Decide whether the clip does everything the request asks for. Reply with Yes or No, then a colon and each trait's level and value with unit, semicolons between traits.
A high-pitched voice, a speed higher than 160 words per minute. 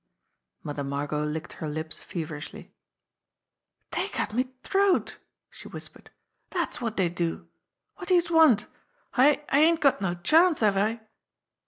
No: high, 215 Hz; average, 150 wpm